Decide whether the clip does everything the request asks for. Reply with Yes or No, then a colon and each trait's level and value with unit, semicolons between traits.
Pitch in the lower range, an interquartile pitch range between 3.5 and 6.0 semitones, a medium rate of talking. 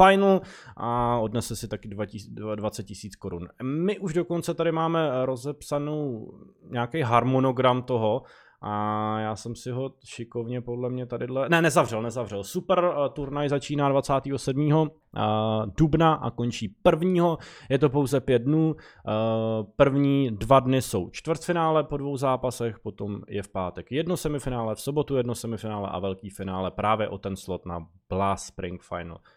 Yes: low, 125 Hz; wide, 5.4 semitones; average, 150 wpm